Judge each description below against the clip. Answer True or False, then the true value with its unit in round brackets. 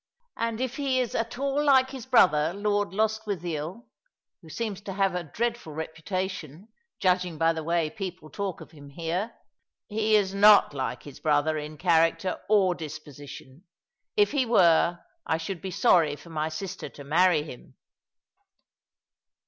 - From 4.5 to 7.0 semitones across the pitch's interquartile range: True (5.2 semitones)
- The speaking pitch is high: False (180 Hz)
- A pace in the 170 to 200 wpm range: False (155 wpm)